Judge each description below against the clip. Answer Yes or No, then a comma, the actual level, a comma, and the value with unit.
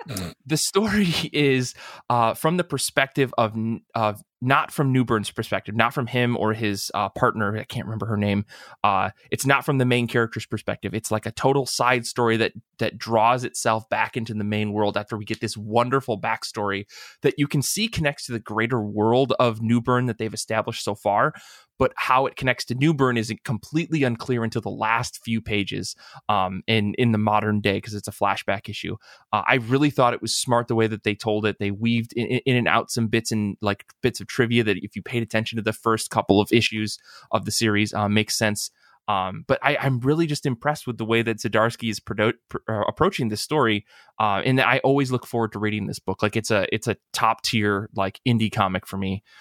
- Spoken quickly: Yes, fast, 215 wpm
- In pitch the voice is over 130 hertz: No, low, 115 Hz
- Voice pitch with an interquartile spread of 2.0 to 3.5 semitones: Yes, average, 3.0 semitones